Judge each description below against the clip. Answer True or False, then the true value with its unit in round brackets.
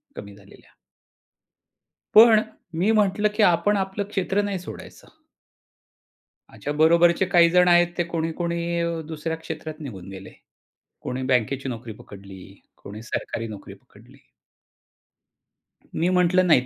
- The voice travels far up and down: True (6.5 semitones)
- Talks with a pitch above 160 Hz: True (170 Hz)